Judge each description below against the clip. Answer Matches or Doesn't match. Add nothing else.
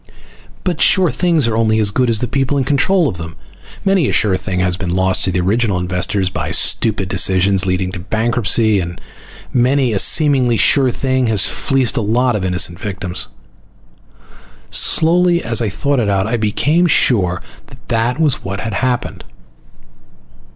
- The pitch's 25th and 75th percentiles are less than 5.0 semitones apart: Doesn't match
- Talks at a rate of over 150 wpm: Matches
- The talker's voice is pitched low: Matches